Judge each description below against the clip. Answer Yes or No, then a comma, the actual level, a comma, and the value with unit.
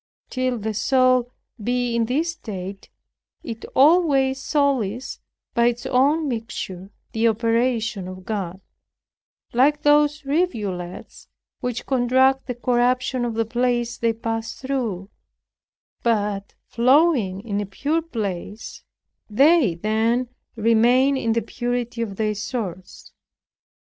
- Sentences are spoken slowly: Yes, slow, 115 wpm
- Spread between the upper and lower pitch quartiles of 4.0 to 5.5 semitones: No, average, 3.4 semitones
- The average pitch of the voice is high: Yes, high, 240 Hz